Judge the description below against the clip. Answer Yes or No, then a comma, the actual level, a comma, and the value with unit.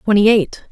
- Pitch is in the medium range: No, high, 210 Hz